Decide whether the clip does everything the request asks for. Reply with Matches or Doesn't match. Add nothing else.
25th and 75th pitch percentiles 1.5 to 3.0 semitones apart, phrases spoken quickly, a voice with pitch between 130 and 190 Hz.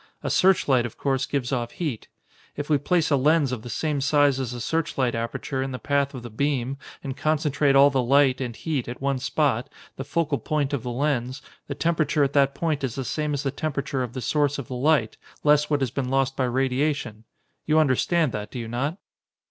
Matches